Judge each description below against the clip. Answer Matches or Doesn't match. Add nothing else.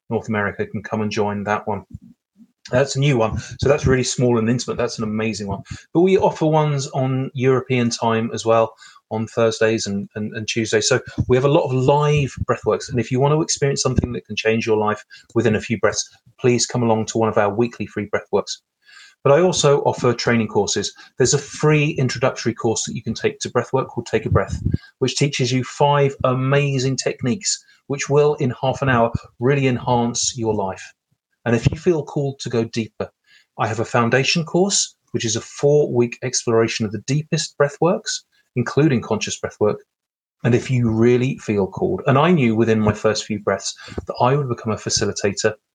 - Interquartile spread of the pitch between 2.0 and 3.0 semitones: Doesn't match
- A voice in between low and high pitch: Doesn't match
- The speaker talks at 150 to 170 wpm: Doesn't match